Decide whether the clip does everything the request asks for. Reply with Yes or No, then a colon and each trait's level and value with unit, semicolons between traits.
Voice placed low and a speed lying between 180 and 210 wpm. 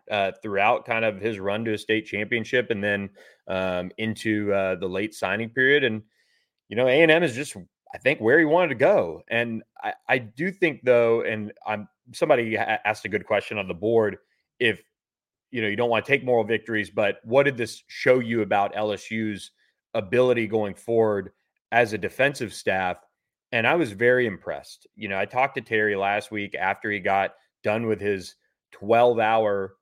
Yes: low, 110 Hz; average, 190 wpm